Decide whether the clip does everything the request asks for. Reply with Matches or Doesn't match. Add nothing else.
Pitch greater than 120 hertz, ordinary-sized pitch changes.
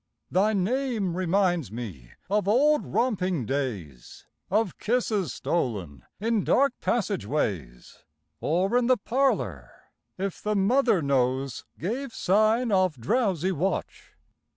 Doesn't match